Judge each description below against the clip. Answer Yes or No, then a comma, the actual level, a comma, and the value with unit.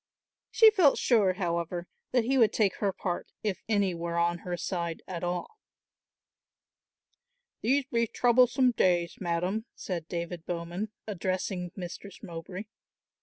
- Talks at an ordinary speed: No, slow, 130 wpm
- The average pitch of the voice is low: No, medium, 185 Hz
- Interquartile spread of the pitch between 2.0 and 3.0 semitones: No, average, 4.3 semitones